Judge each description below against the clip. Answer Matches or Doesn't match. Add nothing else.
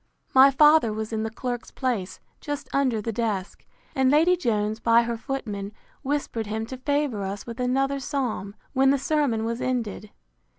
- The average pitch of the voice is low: Doesn't match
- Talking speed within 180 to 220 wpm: Doesn't match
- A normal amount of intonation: Matches